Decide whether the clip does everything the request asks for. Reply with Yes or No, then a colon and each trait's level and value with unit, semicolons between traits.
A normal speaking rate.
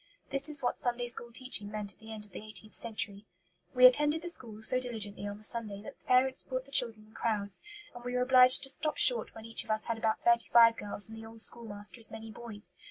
No: fast, 250 wpm